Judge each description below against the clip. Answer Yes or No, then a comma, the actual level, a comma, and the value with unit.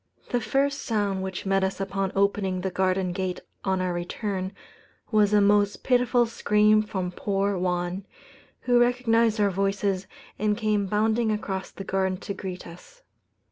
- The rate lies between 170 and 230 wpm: No, average, 155 wpm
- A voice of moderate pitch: No, high, 200 Hz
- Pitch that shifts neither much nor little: No, narrow, 2.2 semitones